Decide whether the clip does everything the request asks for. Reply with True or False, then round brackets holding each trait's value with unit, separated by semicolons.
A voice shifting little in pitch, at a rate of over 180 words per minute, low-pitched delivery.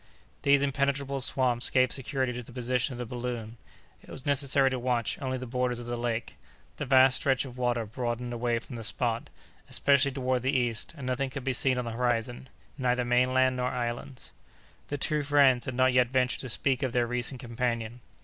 True (1.6 semitones; 200 wpm; 125 Hz)